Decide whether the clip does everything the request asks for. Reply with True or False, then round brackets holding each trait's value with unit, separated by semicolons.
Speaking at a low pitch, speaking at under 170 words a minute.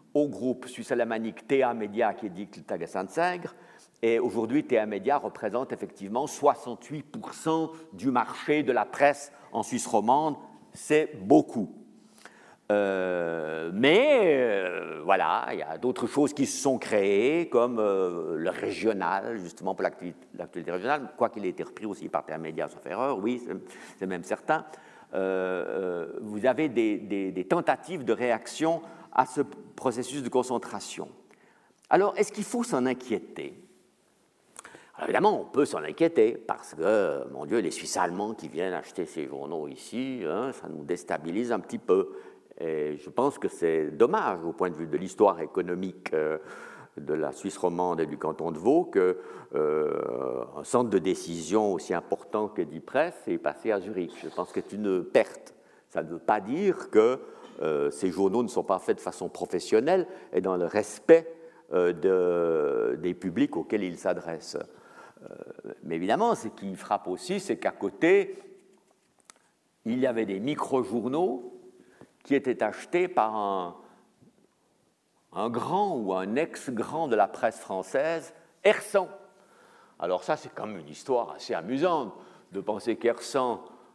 False (165 Hz; 160 wpm)